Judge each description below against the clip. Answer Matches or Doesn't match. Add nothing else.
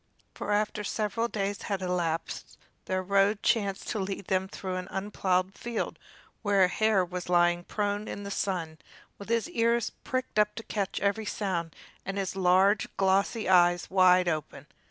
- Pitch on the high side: Matches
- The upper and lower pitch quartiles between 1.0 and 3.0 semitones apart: Matches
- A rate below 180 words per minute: Matches